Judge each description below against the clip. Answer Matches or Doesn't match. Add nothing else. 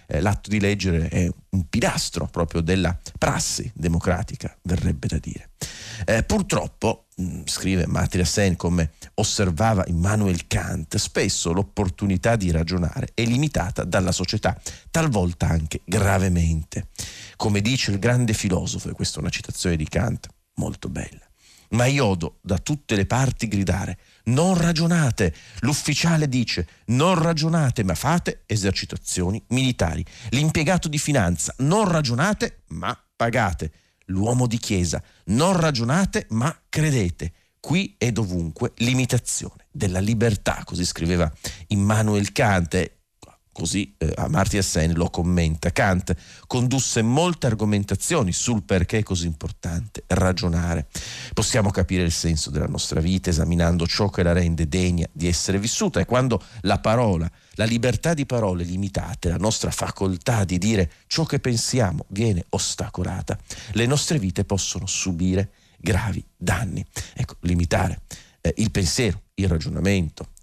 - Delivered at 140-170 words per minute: Doesn't match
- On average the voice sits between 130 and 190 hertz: Doesn't match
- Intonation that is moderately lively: Matches